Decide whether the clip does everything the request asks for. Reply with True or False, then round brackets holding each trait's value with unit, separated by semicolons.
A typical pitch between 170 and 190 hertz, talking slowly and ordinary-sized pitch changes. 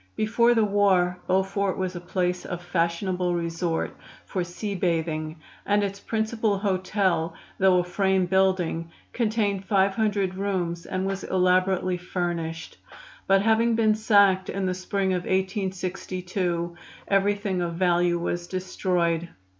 False (185 Hz; 130 wpm; 2.1 semitones)